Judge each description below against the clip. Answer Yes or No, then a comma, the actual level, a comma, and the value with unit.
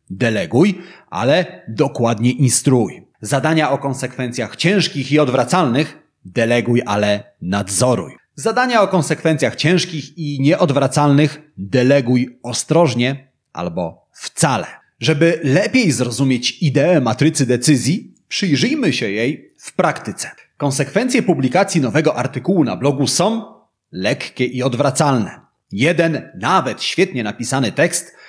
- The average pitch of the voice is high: No, medium, 140 Hz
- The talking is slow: Yes, slow, 105 wpm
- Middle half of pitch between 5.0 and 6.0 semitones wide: No, average, 4.2 semitones